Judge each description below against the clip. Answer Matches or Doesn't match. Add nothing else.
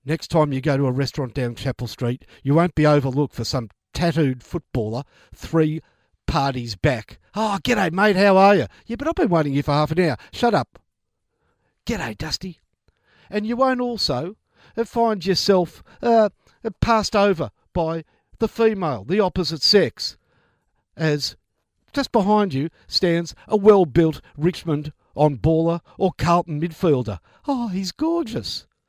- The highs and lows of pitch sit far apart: Matches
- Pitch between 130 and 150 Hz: Doesn't match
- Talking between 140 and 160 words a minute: Matches